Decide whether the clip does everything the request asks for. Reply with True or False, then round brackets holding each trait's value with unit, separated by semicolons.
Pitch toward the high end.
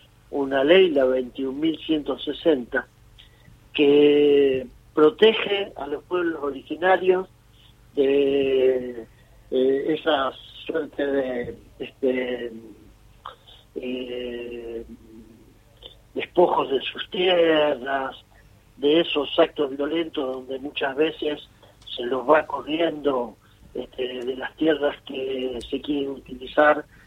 False (135 Hz)